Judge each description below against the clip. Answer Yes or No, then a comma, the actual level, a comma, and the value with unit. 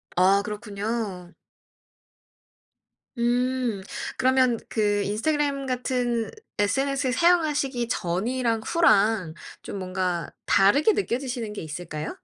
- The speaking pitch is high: Yes, high, 230 Hz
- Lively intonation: No, average, 4.6 semitones